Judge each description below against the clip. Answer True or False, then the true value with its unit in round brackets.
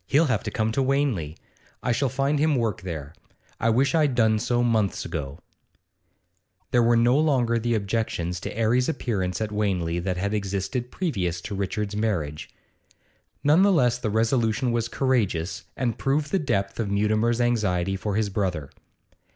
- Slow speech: False (165 wpm)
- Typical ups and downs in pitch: True (4.4 semitones)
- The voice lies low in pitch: True (110 Hz)